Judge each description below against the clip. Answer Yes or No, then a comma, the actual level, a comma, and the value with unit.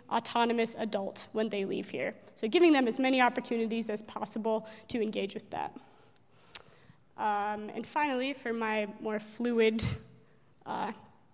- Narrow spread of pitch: Yes, narrow, 2.0 semitones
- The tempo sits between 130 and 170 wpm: Yes, average, 140 wpm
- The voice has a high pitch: Yes, high, 225 Hz